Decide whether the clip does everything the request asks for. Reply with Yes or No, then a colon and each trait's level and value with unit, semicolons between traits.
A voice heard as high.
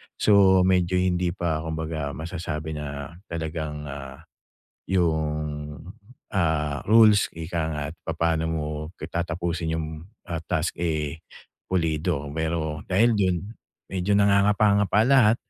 No: very low, 80 Hz